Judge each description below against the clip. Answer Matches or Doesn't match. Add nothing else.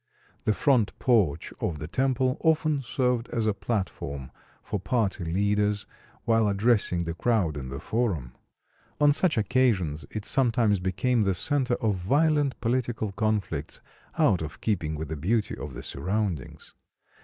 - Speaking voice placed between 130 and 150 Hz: Doesn't match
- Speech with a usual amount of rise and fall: Doesn't match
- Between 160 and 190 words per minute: Doesn't match